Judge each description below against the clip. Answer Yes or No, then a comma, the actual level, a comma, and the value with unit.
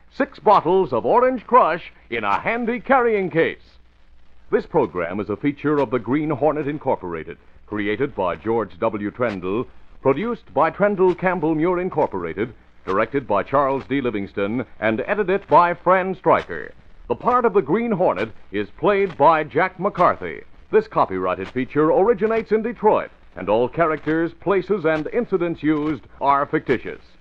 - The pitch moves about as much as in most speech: No, wide, 8.1 semitones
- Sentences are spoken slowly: No, average, 150 wpm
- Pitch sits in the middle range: Yes, medium, 155 Hz